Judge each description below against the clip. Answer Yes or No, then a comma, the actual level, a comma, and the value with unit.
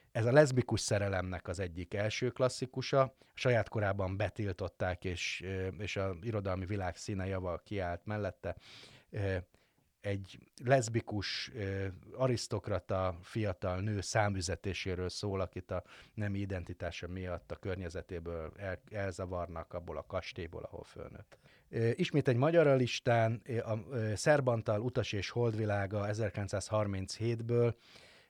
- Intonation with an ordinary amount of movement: Yes, average, 3.6 semitones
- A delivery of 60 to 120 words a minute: Yes, average, 110 wpm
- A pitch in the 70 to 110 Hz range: Yes, low, 105 Hz